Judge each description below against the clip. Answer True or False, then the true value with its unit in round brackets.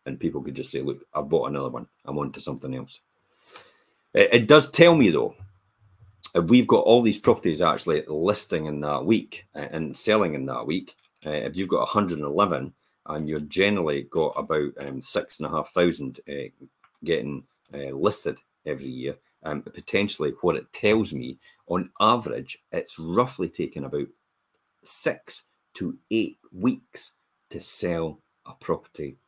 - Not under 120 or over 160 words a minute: True (150 wpm)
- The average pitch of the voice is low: True (85 Hz)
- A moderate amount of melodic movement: False (7.0 semitones)